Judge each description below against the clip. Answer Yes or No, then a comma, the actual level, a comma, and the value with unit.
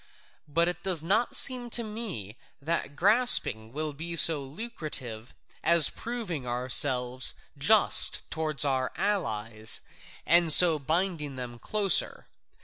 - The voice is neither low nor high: Yes, medium, 155 Hz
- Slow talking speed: Yes, slow, 120 wpm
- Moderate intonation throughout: No, wide, 6.8 semitones